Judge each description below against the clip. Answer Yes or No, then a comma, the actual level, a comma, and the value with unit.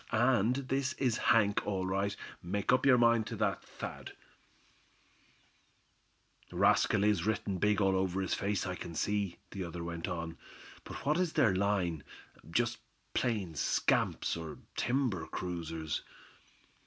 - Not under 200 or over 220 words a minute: No, average, 140 wpm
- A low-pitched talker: Yes, low, 100 Hz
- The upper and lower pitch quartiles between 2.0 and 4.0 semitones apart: No, average, 5.0 semitones